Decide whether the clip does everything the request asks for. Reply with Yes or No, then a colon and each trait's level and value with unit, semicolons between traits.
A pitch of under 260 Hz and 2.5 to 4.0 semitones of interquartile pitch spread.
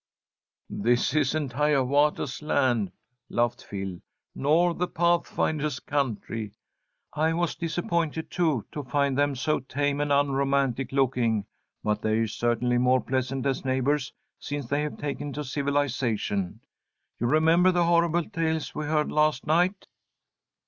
Yes: medium, 140 Hz; average, 3.5 semitones